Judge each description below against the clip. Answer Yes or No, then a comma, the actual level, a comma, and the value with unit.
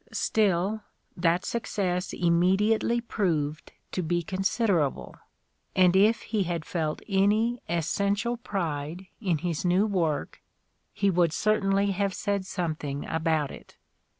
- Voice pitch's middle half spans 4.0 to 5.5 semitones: No, average, 3.4 semitones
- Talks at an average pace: No, slow, 120 wpm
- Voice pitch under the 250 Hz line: Yes, medium, 185 Hz